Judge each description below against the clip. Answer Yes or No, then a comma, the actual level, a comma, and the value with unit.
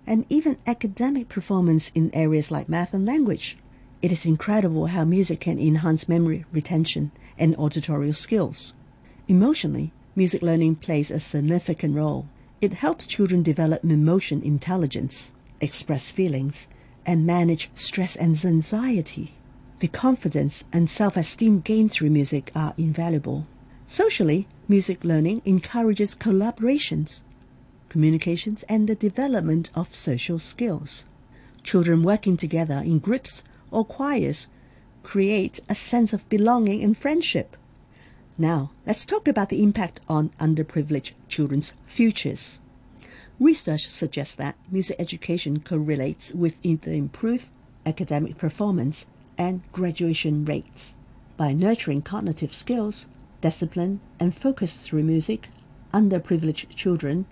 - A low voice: No, medium, 165 Hz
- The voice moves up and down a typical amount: Yes, average, 5.0 semitones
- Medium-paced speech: No, slow, 115 wpm